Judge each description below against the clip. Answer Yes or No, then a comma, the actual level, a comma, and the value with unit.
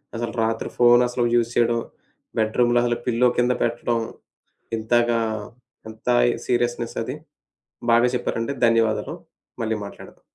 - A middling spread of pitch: No, narrow, 0.9 semitones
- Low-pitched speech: Yes, low, 120 Hz